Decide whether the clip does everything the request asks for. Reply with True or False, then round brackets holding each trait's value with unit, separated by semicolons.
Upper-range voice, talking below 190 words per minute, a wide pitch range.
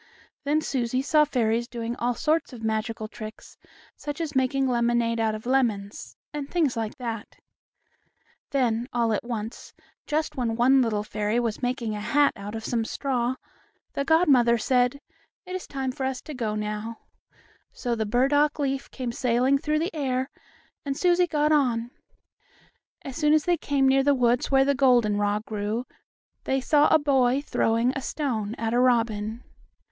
False (250 Hz; 165 wpm; 3.6 semitones)